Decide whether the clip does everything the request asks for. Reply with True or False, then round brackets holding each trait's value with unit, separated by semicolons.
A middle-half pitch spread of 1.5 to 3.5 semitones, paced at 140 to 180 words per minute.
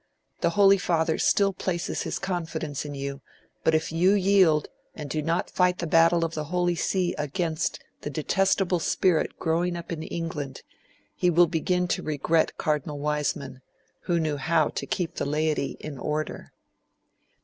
True (2.8 semitones; 160 wpm)